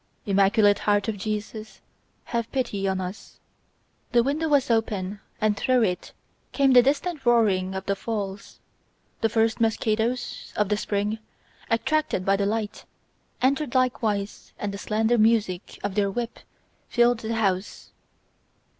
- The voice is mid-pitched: No, high, 220 Hz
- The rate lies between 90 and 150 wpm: Yes, average, 140 wpm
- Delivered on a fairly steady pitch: No, average, 3.0 semitones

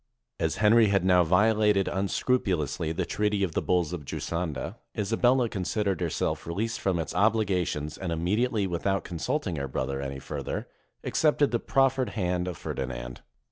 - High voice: No, very low, 95 Hz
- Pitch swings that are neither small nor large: Yes, average, 4.7 semitones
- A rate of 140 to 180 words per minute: Yes, average, 160 wpm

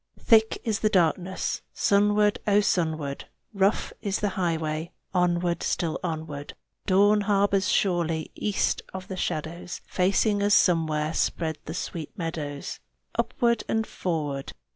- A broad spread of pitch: No, average, 4.2 semitones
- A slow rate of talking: Yes, slow, 125 wpm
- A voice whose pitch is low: No, medium, 180 Hz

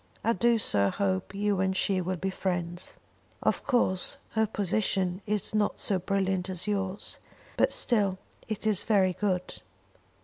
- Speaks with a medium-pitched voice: No, high, 195 Hz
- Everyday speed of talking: Yes, average, 150 wpm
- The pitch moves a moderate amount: No, narrow, 2.1 semitones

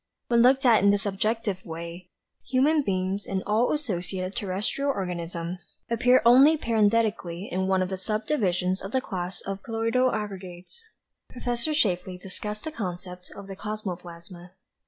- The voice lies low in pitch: No, high, 200 Hz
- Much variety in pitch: No, average, 4.1 semitones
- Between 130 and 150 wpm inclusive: Yes, average, 145 wpm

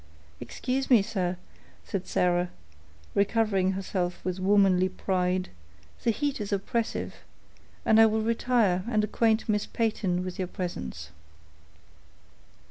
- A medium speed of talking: No, slow, 120 wpm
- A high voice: Yes, high, 195 Hz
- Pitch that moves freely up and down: No, average, 3.4 semitones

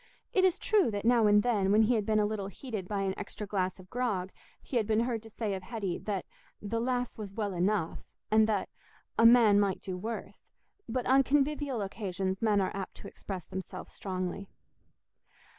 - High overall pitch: Yes, high, 210 Hz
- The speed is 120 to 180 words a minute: No, average, 200 wpm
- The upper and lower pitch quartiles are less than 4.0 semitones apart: Yes, average, 3.1 semitones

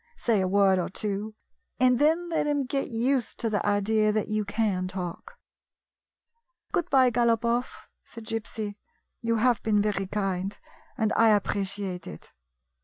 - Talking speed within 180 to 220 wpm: No, average, 150 wpm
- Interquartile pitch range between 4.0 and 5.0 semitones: No, average, 3.0 semitones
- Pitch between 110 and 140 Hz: No, high, 215 Hz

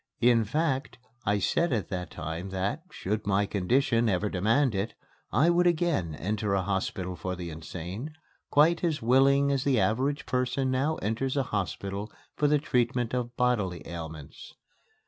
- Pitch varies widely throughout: Yes, wide, 6.1 semitones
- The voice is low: Yes, low, 115 Hz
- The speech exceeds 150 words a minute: Yes, average, 160 wpm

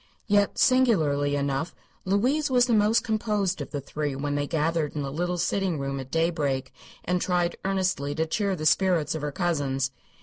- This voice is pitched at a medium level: Yes, medium, 165 Hz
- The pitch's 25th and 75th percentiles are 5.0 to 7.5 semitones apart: Yes, wide, 5.5 semitones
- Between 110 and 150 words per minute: No, average, 180 wpm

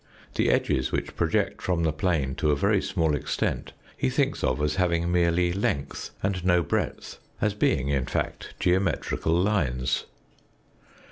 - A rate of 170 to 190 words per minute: No, average, 150 wpm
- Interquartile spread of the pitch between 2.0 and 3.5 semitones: No, average, 3.9 semitones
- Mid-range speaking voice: No, very low, 85 Hz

